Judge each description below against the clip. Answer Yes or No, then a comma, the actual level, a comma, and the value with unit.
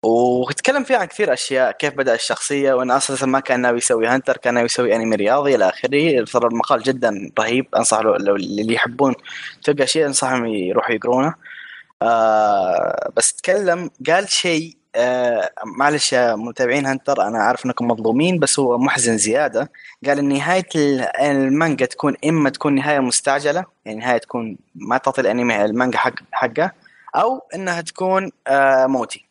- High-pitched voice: No, low, 135 Hz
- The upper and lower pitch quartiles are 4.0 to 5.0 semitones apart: No, average, 3.5 semitones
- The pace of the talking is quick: Yes, fast, 160 wpm